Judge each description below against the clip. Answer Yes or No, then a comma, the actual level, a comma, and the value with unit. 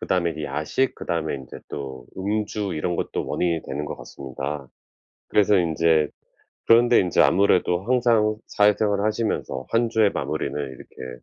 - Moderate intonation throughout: No, wide, 6.3 semitones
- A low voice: Yes, very low, 90 Hz